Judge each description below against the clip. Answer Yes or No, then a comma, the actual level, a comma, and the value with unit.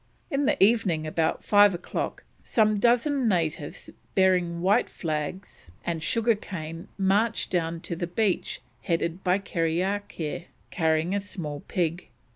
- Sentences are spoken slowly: Yes, slow, 130 wpm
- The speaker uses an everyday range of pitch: Yes, average, 3.7 semitones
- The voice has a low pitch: No, medium, 180 Hz